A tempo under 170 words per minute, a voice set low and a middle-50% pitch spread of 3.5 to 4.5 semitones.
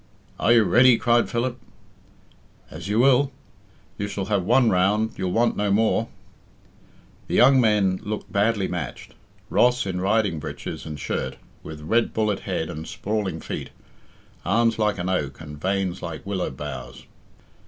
Yes: average, 155 wpm; low, 105 Hz; average, 4.0 semitones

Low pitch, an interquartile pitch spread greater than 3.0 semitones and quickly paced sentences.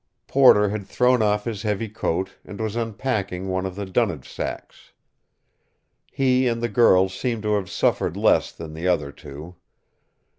No: low, 105 Hz; average, 3.8 semitones; average, 160 wpm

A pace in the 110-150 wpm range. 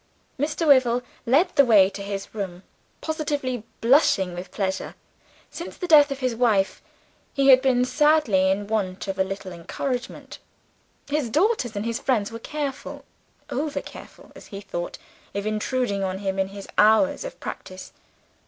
No: average, 160 wpm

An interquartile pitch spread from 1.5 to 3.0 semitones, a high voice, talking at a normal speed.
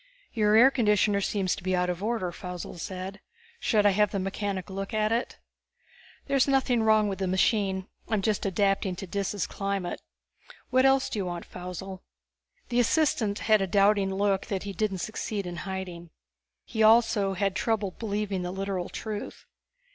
Yes: narrow, 2.4 semitones; high, 200 Hz; average, 170 wpm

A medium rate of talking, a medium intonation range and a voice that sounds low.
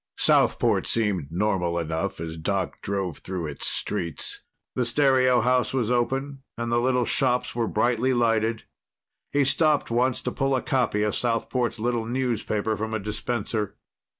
Yes: average, 150 wpm; average, 3.8 semitones; low, 115 Hz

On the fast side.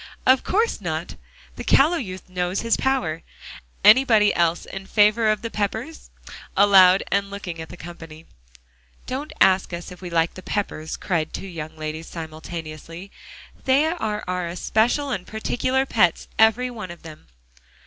No: average, 155 wpm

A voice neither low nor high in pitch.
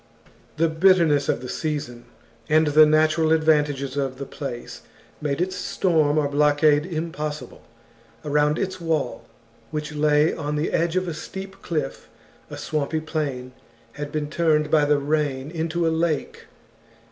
Yes: medium, 150 Hz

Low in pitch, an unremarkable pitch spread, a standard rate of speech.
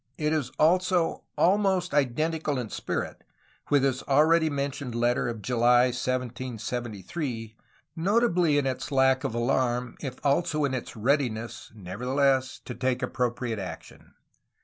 No: low, 130 Hz; average, 4.0 semitones; slow, 125 wpm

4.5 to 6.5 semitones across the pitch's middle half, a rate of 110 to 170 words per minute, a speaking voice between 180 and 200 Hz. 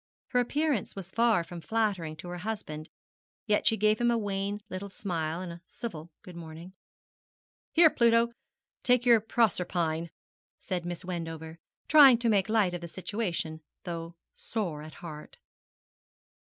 Yes: average, 5.1 semitones; average, 150 wpm; medium, 185 Hz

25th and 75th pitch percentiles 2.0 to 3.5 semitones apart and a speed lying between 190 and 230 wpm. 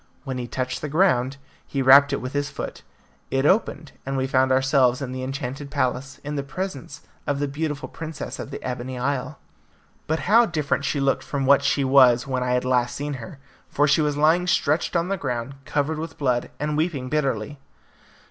Yes: narrow, 2.6 semitones; average, 200 wpm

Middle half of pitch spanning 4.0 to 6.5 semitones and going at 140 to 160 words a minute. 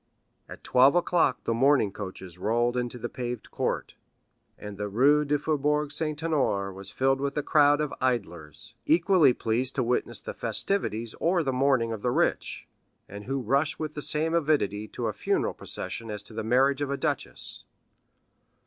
No: average, 4.9 semitones; average, 175 wpm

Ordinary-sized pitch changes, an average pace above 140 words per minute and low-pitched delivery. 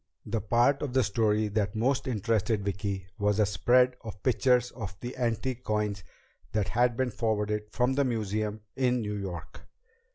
Yes: average, 3.1 semitones; average, 165 wpm; low, 110 Hz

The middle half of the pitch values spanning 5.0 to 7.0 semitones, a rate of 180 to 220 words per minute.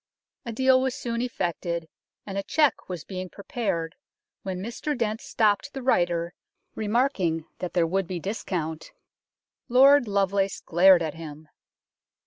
No: wide, 5.6 semitones; slow, 135 wpm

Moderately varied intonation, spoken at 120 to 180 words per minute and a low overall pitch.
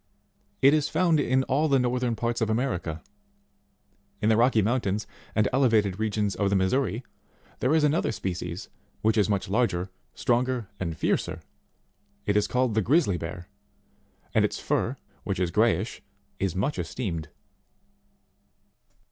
Yes: average, 5.0 semitones; average, 145 wpm; low, 110 Hz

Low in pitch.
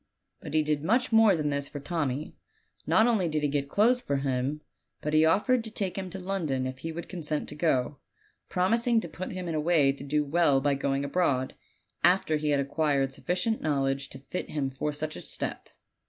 No: medium, 150 Hz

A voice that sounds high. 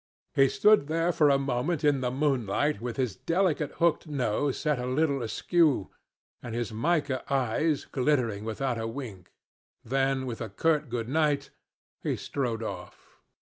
No: low, 135 Hz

